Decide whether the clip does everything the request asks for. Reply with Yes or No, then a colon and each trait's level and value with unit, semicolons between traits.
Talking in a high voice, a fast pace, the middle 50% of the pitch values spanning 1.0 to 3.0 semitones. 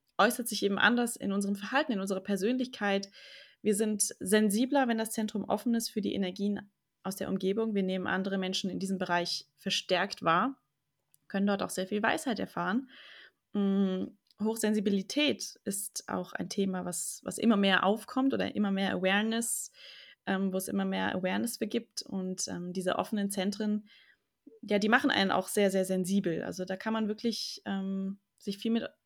No: high, 200 Hz; average, 175 wpm; average, 2.7 semitones